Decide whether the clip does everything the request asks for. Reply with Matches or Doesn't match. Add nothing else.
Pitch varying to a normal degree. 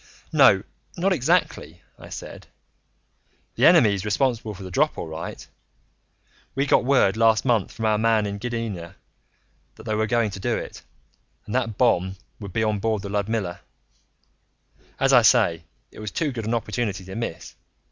Matches